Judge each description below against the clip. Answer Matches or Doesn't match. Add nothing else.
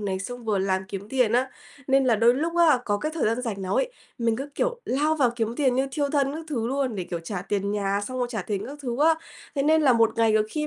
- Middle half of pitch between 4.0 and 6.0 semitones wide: Matches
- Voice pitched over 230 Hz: Matches